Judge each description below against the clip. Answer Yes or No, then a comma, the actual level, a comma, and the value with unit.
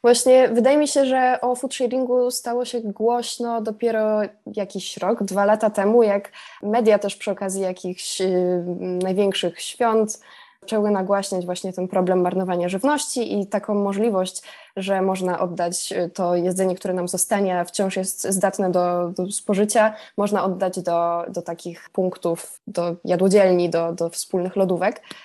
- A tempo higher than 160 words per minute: No, average, 145 wpm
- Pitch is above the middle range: Yes, high, 195 Hz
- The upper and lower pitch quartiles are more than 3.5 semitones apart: No, average, 3.2 semitones